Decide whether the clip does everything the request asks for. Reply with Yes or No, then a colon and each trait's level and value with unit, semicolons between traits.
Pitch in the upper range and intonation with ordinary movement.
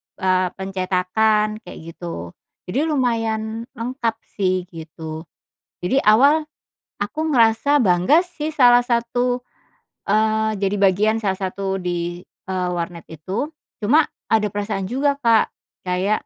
Yes: high, 210 Hz; average, 4.3 semitones